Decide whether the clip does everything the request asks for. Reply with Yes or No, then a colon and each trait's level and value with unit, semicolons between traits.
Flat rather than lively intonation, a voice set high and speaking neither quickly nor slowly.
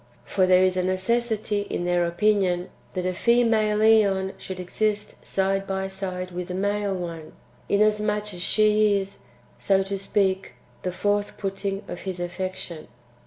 Yes: narrow, 2.3 semitones; high, 195 Hz; average, 155 wpm